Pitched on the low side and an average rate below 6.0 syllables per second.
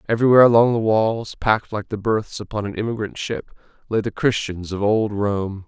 Yes: low, 110 Hz; 5.5 syllables/s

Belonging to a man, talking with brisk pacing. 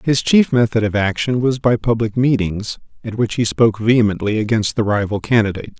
No: male; average, 185 wpm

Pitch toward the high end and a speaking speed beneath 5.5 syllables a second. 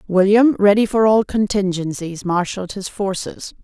Yes: high, 200 Hz; 4.7 syllables/s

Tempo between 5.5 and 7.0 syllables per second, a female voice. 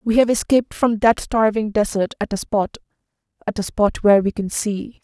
No: 5.2 syllables/s; female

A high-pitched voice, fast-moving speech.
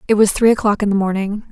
Yes: high, 205 Hz; fast, 275 wpm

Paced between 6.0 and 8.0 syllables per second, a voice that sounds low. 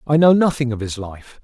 No: 5.4 syllables/s; low, 130 Hz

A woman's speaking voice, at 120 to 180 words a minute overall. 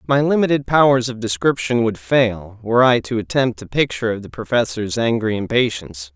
No: male; average, 175 wpm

